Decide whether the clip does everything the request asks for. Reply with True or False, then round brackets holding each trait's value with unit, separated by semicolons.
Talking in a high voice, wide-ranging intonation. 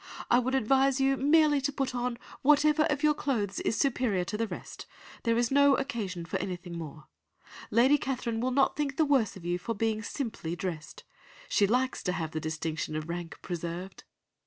True (230 Hz; 7.3 semitones)